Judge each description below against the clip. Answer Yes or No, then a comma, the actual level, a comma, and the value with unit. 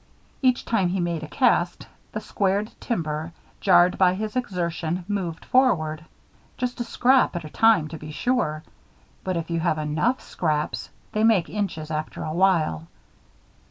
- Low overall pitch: No, medium, 175 Hz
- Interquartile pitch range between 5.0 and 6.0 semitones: Yes, average, 5.3 semitones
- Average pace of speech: Yes, average, 160 wpm